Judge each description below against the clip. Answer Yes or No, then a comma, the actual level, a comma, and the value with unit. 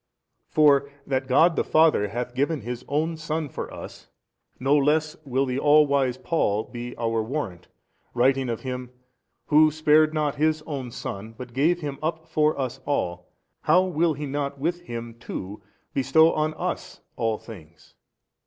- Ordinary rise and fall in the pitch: Yes, average, 4.1 semitones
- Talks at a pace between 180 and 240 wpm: No, average, 160 wpm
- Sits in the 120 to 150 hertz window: Yes, medium, 140 Hz